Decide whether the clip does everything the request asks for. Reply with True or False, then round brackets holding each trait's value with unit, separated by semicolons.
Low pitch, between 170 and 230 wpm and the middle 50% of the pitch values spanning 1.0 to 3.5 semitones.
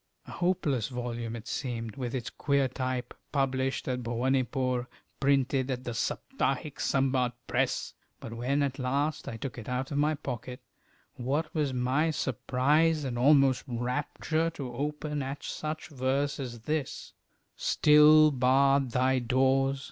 False (130 Hz; 140 wpm; 2.5 semitones)